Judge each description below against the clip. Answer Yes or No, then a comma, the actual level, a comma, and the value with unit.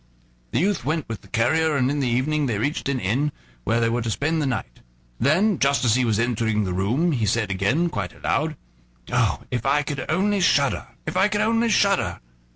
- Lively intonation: Yes, wide, 5.7 semitones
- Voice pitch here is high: No, medium, 140 Hz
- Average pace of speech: No, fast, 215 wpm